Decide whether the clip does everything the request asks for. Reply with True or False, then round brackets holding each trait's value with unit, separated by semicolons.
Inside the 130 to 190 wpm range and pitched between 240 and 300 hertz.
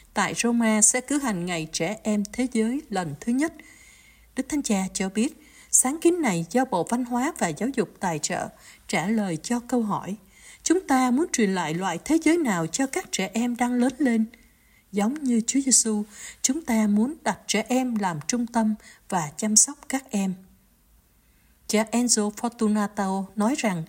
False (185 wpm; 225 Hz)